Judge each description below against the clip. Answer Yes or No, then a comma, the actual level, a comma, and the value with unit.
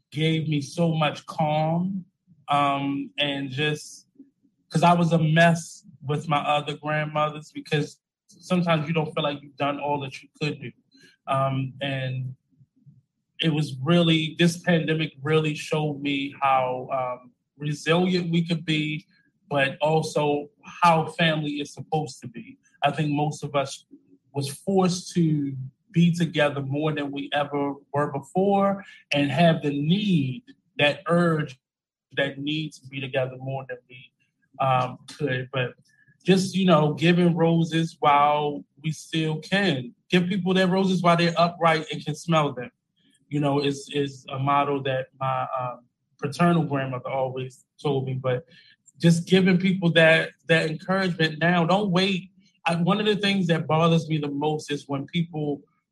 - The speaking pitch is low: No, medium, 150 Hz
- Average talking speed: Yes, average, 155 wpm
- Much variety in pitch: No, average, 3.2 semitones